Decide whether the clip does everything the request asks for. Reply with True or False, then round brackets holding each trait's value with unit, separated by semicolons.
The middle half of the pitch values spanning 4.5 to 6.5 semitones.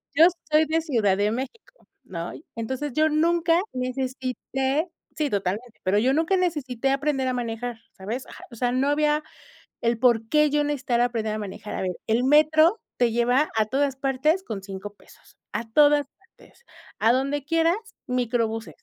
True (4.8 semitones)